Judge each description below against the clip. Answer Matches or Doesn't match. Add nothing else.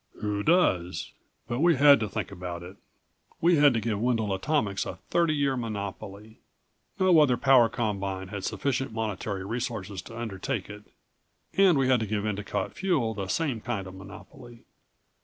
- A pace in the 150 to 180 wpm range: Matches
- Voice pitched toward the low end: Matches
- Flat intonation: Doesn't match